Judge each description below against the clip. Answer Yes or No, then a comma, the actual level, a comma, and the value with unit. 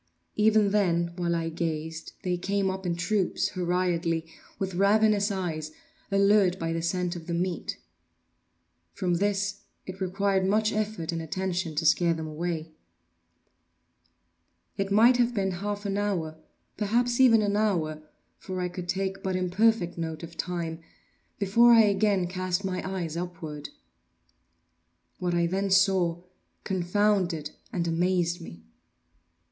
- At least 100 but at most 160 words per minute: Yes, average, 140 wpm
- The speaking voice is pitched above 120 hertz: Yes, medium, 185 Hz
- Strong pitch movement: No, average, 3.0 semitones